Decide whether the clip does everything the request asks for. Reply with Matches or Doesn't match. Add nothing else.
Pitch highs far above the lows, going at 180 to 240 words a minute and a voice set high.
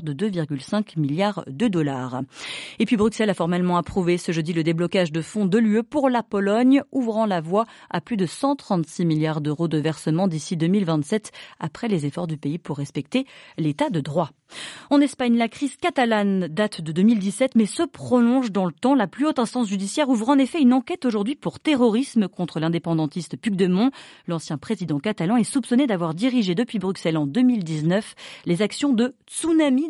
Matches